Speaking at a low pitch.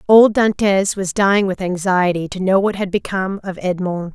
No: high, 190 Hz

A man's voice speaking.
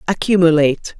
No: female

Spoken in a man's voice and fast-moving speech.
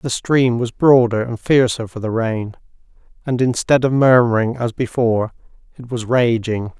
No: male; average, 160 wpm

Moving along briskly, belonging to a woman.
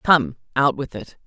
No: average, 190 wpm; female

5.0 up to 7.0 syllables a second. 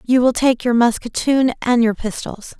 No: 4.4 syllables/s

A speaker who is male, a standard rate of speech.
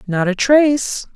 No: female; average, 155 wpm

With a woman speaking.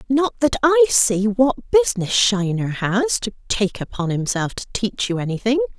Yes: female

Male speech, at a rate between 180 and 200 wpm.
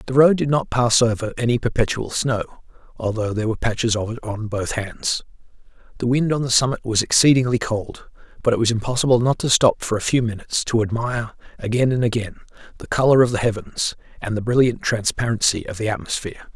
Yes: male; average, 195 wpm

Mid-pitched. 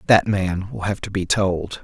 No: very low, 95 Hz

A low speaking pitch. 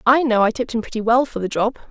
No: high, 230 Hz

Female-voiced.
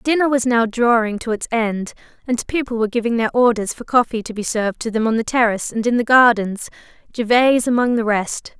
Yes: female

